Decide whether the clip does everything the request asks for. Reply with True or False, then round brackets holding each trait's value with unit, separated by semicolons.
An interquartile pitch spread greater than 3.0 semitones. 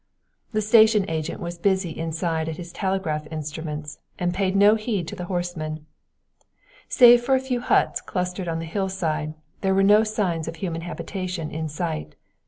True (3.7 semitones)